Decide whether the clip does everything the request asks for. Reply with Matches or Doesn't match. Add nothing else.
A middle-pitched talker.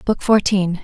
Doesn't match